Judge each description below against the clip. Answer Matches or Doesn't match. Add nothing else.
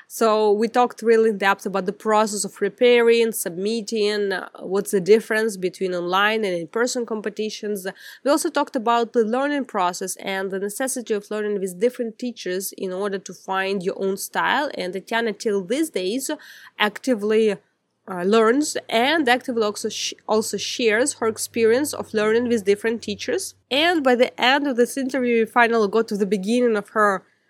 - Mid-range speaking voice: Doesn't match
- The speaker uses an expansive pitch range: Doesn't match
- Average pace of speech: Matches